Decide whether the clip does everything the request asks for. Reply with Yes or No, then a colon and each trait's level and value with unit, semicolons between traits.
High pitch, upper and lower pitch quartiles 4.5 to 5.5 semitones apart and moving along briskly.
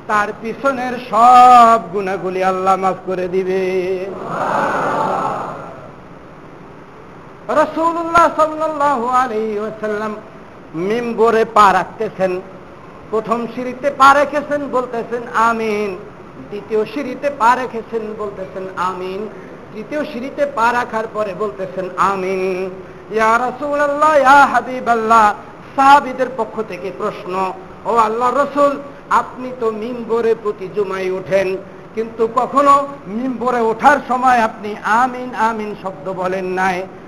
No: high, 220 Hz; average, 4.9 semitones; average, 100 wpm